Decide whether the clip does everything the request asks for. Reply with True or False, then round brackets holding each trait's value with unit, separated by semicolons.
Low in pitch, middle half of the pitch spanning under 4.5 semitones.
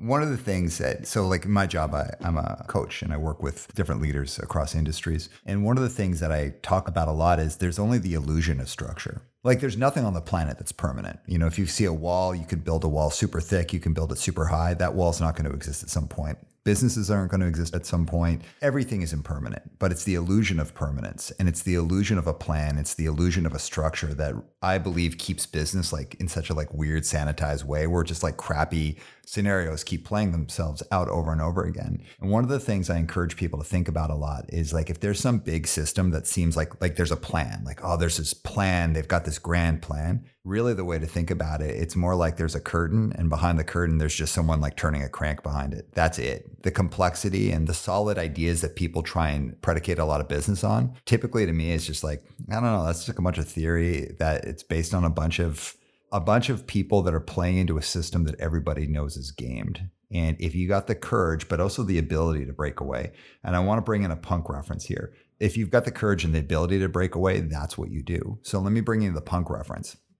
True (85 Hz; 3.5 semitones)